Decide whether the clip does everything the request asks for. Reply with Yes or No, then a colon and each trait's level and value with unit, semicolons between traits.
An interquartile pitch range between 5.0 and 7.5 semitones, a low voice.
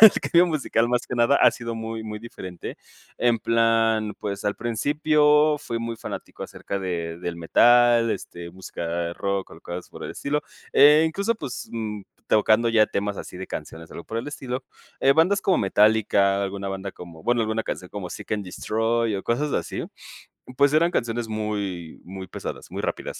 No: average, 4.0 semitones; low, 110 Hz